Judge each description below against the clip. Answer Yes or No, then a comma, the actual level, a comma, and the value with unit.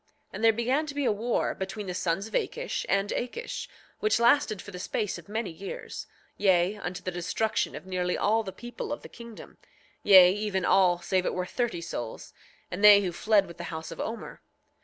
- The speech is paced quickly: Yes, fast, 210 wpm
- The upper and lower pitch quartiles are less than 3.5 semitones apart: No, average, 3.8 semitones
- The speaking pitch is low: No, high, 200 Hz